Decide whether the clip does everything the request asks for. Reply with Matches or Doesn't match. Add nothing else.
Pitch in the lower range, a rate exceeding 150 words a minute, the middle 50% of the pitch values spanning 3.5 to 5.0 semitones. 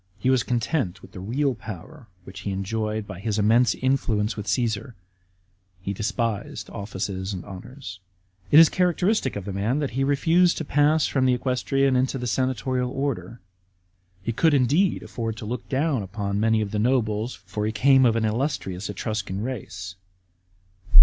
Matches